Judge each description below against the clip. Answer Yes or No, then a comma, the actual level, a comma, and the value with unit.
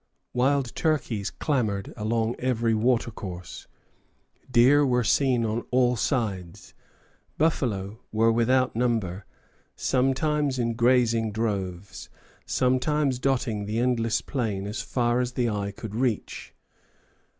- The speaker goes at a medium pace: No, slow, 115 wpm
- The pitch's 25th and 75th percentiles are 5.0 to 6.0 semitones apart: No, average, 3.0 semitones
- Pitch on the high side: No, low, 120 Hz